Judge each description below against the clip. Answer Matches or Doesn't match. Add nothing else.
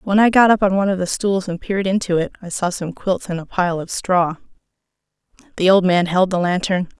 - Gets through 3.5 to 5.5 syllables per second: Doesn't match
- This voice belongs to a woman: Matches